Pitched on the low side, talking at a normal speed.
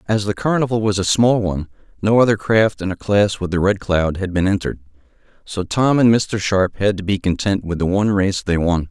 No: low, 100 Hz; fast, 235 wpm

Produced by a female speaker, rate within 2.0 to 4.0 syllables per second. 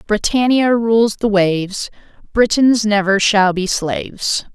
Yes: female; 3.8 syllables/s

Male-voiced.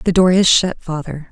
No: female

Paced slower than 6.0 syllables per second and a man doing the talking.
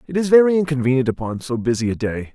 No: 6.8 syllables/s; male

